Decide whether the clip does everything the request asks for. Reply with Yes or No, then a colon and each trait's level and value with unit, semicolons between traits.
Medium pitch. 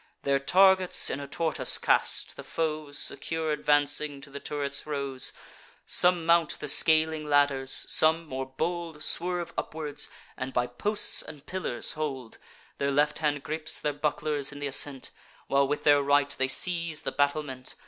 Yes: medium, 145 Hz